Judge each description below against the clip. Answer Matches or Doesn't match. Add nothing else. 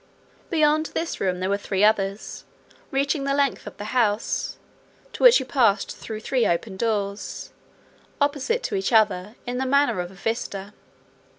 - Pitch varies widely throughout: Matches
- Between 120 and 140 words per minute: Doesn't match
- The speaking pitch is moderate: Doesn't match